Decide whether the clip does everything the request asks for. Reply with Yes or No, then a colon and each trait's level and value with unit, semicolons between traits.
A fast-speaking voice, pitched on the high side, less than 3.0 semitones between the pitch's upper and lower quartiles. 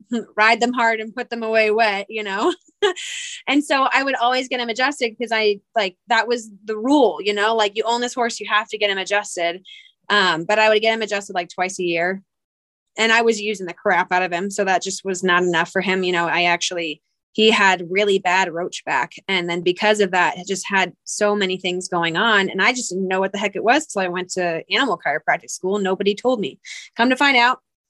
No: fast, 245 wpm; high, 205 Hz; average, 3.9 semitones